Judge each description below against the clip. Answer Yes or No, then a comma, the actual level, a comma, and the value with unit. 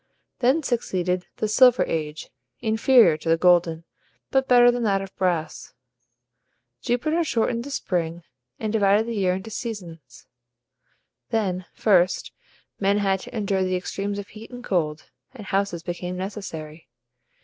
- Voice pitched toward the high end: Yes, high, 195 Hz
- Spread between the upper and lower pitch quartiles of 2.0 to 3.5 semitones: No, average, 4.2 semitones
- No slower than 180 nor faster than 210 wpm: No, average, 140 wpm